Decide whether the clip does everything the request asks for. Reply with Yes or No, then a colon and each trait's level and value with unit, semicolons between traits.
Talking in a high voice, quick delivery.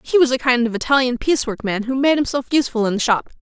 Yes: very high, 255 Hz; fast, 280 wpm